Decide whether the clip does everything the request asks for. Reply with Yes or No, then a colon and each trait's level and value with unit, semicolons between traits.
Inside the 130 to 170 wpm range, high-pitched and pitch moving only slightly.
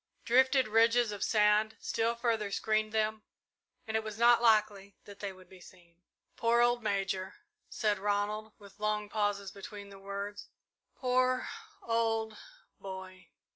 Yes: average, 140 wpm; high, 215 Hz; narrow, 2.2 semitones